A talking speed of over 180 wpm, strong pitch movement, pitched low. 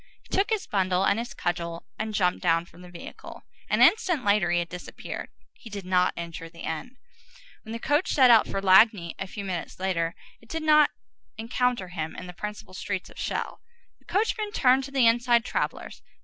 No: average, 200 wpm; wide, 5.7 semitones; high, 200 Hz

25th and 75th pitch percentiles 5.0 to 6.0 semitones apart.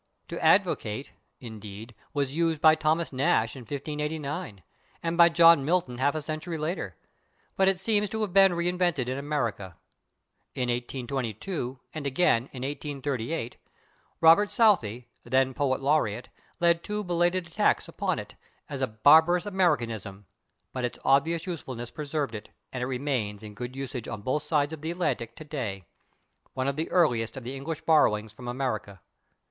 Yes: wide, 5.4 semitones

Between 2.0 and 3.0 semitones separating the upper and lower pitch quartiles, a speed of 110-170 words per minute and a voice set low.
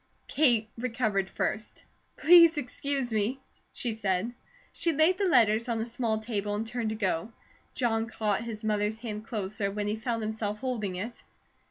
No: narrow, 2.6 semitones; average, 165 wpm; high, 225 Hz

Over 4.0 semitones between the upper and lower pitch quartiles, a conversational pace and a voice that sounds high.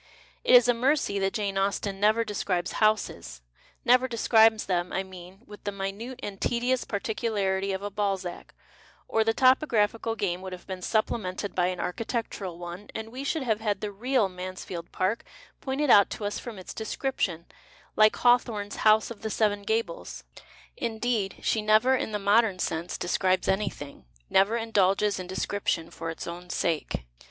No: average, 3.3 semitones; average, 180 wpm; high, 205 Hz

